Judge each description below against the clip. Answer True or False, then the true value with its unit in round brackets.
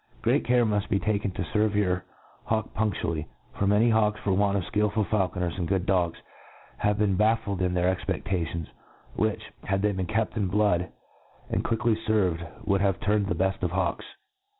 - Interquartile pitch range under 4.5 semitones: True (2.6 semitones)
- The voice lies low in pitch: True (100 Hz)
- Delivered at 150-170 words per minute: False (185 wpm)